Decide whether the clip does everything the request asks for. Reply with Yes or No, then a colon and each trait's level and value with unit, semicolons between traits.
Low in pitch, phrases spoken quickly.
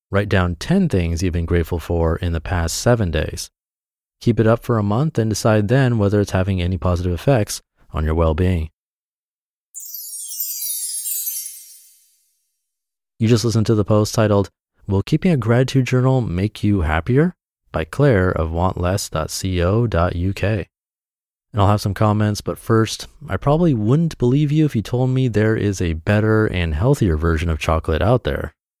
No: low, 105 Hz; average, 165 wpm